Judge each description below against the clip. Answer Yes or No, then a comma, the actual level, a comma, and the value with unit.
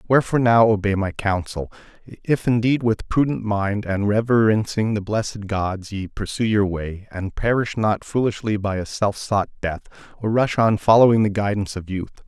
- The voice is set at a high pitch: No, low, 105 Hz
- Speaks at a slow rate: No, average, 175 wpm